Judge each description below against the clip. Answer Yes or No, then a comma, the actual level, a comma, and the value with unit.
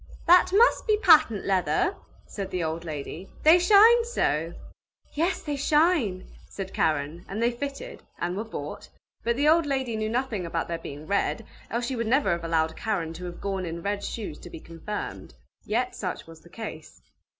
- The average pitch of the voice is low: No, high, 205 Hz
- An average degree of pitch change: No, wide, 8.6 semitones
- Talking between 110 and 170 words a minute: No, average, 185 wpm